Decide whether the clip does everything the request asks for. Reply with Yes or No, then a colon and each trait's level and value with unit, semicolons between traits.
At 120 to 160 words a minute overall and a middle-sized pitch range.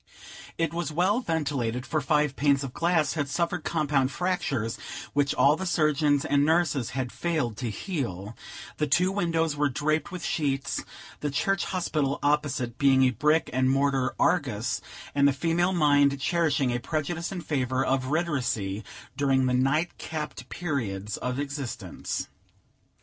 Yes: average, 150 wpm; average, 3.7 semitones